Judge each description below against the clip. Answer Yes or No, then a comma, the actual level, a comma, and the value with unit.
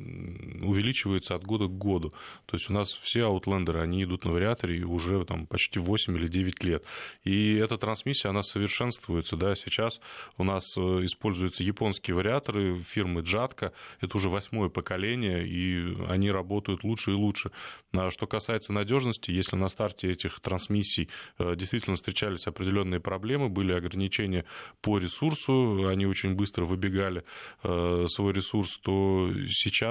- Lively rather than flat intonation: No, narrow, 2.5 semitones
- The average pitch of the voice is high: No, very low, 95 Hz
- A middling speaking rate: Yes, average, 140 wpm